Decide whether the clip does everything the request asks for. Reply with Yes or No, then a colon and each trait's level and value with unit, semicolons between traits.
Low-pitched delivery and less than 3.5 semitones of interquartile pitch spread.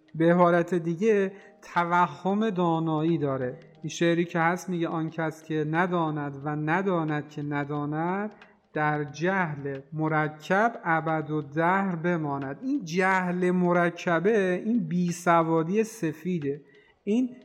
No: medium, 170 Hz; average, 2.9 semitones